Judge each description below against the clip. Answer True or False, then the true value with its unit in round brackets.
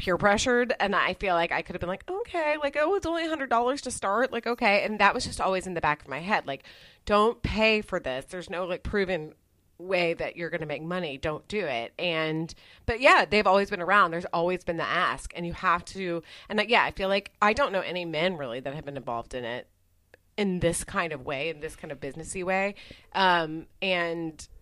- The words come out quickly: True (245 wpm)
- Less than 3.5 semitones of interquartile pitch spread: False (4.2 semitones)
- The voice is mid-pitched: True (180 Hz)